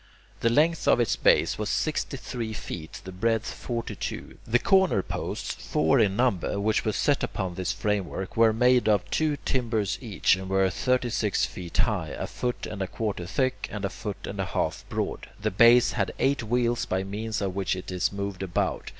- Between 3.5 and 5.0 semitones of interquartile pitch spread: Yes, average, 4.0 semitones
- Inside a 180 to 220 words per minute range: Yes, average, 200 wpm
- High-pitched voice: No, low, 105 Hz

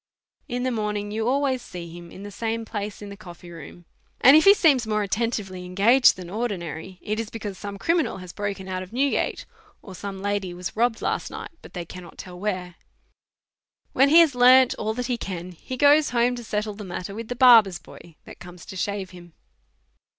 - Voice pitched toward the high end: Yes, high, 205 Hz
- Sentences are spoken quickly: Yes, fast, 210 wpm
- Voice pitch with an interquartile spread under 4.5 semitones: No, average, 4.8 semitones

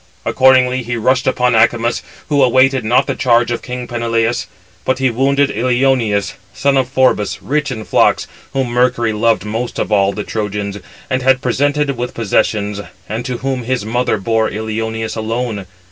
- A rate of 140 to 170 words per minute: Yes, average, 165 wpm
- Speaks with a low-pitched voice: Yes, low, 120 Hz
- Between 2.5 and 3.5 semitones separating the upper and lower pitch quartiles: Yes, average, 2.8 semitones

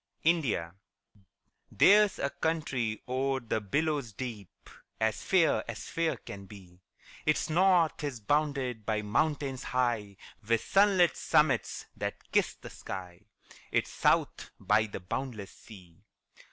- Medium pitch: No, low, 125 Hz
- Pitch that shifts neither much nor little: No, wide, 6.7 semitones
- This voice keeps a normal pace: No, slow, 125 wpm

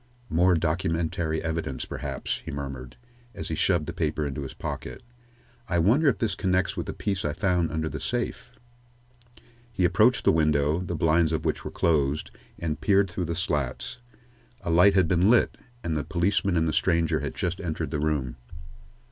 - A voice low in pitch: Yes, very low, 80 Hz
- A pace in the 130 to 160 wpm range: No, average, 180 wpm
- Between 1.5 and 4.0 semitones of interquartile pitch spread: Yes, average, 3.0 semitones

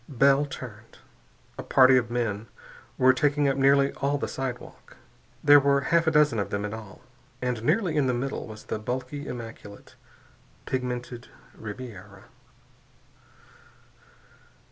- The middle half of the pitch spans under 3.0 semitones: No, average, 3.3 semitones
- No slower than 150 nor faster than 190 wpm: No, slow, 135 wpm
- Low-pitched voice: Yes, low, 130 Hz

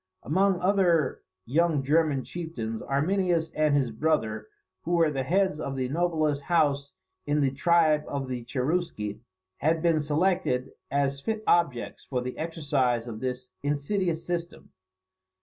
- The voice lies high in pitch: No, medium, 150 Hz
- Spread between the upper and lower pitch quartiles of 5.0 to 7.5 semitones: No, average, 4.2 semitones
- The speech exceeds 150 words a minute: No, average, 140 wpm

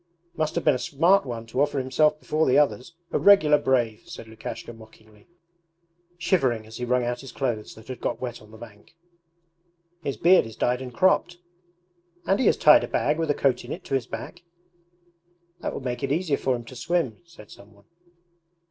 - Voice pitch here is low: Yes, low, 130 Hz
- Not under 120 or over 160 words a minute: No, fast, 205 wpm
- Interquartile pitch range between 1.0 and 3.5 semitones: No, average, 4.8 semitones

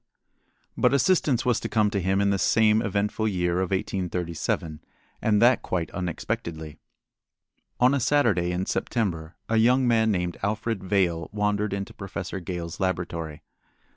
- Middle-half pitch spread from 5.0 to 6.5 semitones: No, average, 4.1 semitones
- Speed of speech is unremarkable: Yes, average, 145 wpm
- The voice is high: No, low, 100 Hz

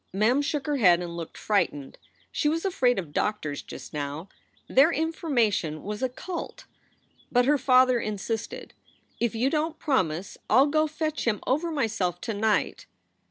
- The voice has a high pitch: Yes, high, 240 Hz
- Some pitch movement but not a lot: No, wide, 7.3 semitones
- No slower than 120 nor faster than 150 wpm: No, average, 160 wpm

